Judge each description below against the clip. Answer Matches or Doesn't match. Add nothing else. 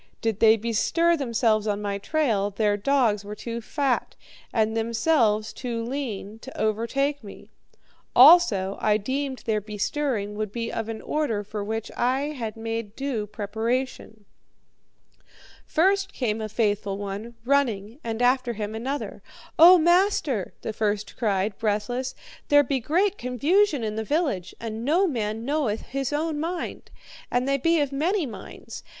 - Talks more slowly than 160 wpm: Matches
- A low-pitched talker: Doesn't match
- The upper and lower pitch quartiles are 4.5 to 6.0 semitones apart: Matches